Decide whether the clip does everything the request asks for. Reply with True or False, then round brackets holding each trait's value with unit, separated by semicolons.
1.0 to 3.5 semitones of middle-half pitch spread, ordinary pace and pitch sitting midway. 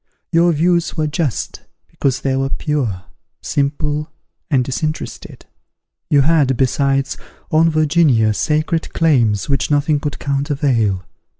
False (2.7 semitones; 115 wpm; 145 Hz)